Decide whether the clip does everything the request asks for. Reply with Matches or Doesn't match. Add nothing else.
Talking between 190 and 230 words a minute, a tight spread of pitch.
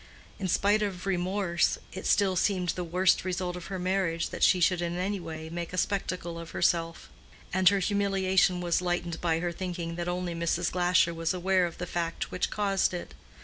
Matches